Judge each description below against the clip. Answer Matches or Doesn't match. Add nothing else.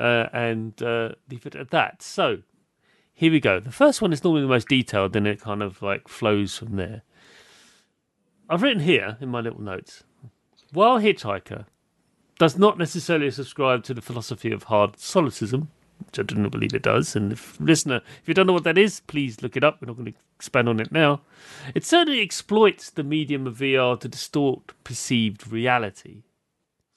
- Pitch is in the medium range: Doesn't match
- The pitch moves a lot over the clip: Matches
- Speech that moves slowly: Doesn't match